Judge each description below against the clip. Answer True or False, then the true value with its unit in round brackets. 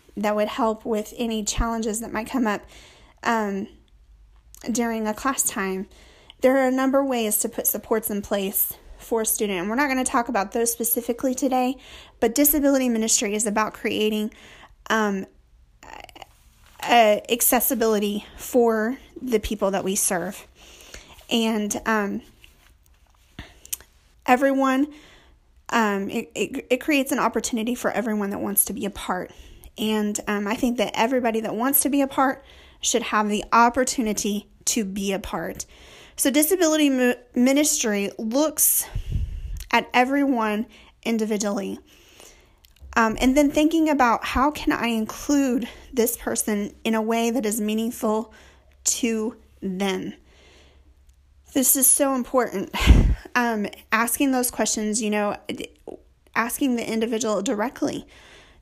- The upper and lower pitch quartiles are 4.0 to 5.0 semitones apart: False (3.4 semitones)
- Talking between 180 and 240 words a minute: False (135 wpm)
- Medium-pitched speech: False (225 Hz)